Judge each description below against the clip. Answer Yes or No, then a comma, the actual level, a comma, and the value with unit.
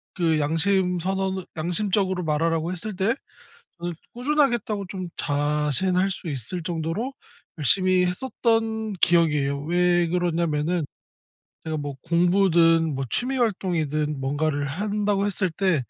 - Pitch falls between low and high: Yes, medium, 175 Hz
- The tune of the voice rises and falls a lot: No, average, 3.7 semitones